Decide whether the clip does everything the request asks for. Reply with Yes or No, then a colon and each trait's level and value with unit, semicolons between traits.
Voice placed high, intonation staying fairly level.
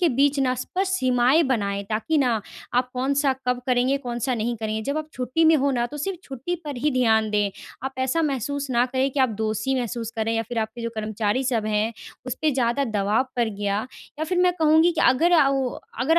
No: very high, 255 Hz; average, 3.8 semitones